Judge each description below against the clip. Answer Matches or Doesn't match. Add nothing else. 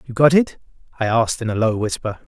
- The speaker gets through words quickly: Matches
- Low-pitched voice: Matches